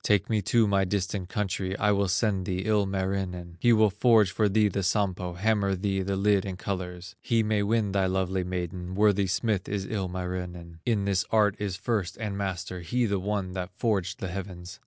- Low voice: Yes, very low, 95 Hz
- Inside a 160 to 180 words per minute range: No, average, 195 wpm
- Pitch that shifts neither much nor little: No, narrow, 2.2 semitones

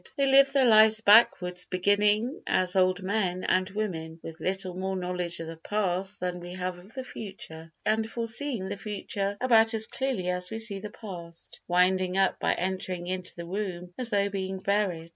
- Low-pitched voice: No, high, 190 Hz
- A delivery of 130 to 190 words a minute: Yes, average, 185 wpm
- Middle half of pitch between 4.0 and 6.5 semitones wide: No, average, 3.1 semitones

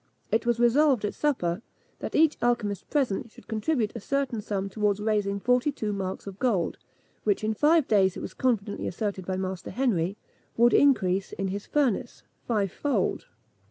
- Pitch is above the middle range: Yes, high, 215 Hz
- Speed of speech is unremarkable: Yes, average, 165 wpm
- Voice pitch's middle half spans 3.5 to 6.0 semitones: Yes, average, 4.1 semitones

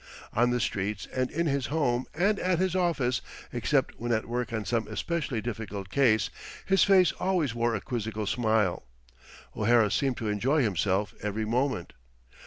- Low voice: Yes, low, 120 Hz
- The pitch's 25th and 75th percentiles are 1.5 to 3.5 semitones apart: No, average, 4.8 semitones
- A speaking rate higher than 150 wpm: Yes, average, 165 wpm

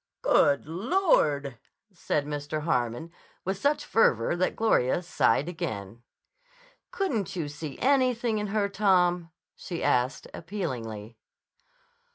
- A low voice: No, medium, 170 Hz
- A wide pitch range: Yes, wide, 6.8 semitones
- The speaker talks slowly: Yes, slow, 110 wpm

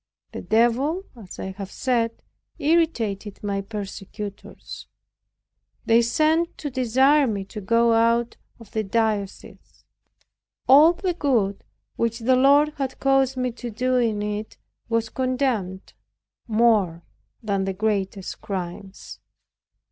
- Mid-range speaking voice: No, high, 230 Hz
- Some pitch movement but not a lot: Yes, average, 4.3 semitones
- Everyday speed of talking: No, slow, 120 wpm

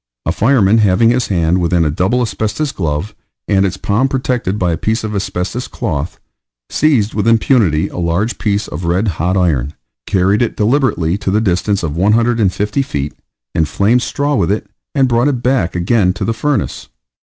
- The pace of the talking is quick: No, average, 175 wpm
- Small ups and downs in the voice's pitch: No, average, 4.8 semitones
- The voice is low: Yes, low, 100 Hz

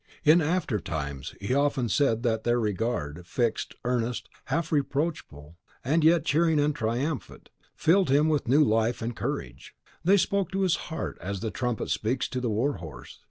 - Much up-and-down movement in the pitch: Yes, wide, 5.7 semitones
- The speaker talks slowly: No, average, 165 wpm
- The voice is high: No, low, 125 Hz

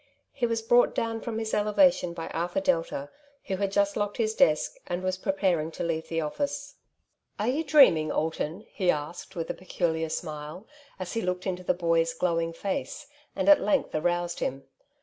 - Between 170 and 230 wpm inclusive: Yes, average, 195 wpm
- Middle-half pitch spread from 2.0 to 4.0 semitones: No, average, 5.1 semitones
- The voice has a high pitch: No, medium, 180 Hz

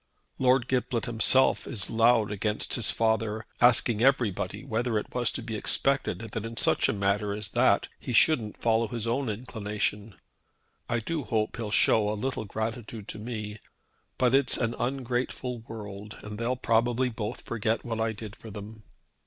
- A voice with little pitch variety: Yes, narrow, 2.3 semitones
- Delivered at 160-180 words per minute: Yes, average, 170 wpm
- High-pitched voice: No, low, 115 Hz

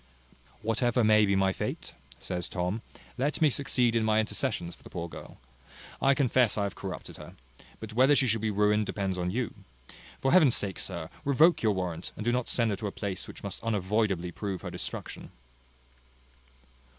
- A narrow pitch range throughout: No, average, 4.2 semitones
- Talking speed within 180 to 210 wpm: Yes, average, 185 wpm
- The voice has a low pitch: Yes, low, 110 Hz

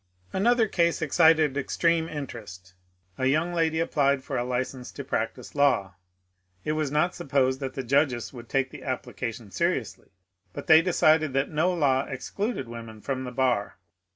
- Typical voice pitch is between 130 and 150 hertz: Yes, medium, 140 Hz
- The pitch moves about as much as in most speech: Yes, average, 4.1 semitones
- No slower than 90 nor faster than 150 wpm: No, average, 165 wpm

